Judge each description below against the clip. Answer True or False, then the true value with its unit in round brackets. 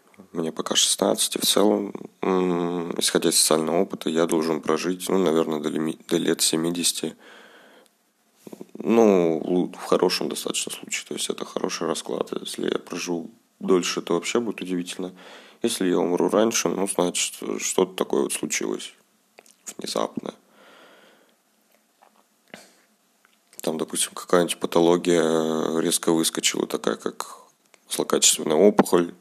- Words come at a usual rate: True (120 wpm)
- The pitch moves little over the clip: True (2.2 semitones)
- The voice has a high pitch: False (85 Hz)